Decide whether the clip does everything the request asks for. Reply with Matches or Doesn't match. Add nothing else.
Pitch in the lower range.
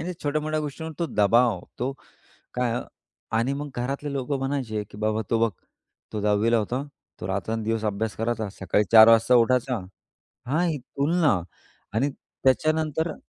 Matches